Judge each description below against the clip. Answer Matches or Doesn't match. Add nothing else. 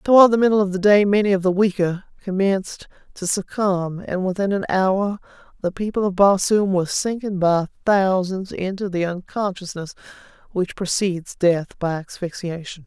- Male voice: Doesn't match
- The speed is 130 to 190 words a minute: Matches